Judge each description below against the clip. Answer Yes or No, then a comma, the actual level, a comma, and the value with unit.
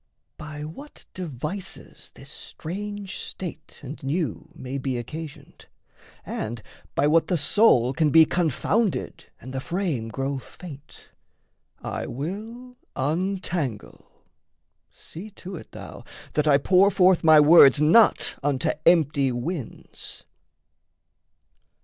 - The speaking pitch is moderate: Yes, medium, 155 Hz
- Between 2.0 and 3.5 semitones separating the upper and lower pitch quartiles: No, average, 5.1 semitones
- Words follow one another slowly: Yes, slow, 115 wpm